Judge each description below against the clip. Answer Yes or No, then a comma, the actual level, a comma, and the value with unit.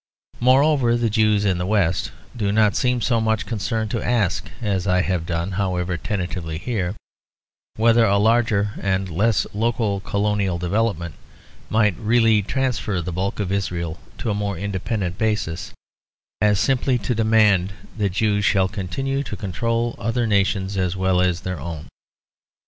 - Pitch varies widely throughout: No, average, 3.5 semitones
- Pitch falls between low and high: No, low, 100 Hz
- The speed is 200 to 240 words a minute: No, average, 155 wpm